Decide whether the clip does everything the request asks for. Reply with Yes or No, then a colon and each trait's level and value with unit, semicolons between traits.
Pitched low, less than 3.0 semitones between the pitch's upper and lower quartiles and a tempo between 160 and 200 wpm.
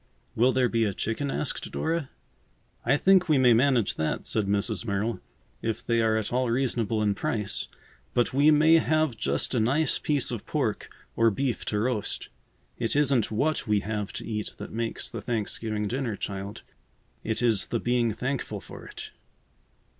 No: low, 115 Hz; average, 3.7 semitones; average, 175 wpm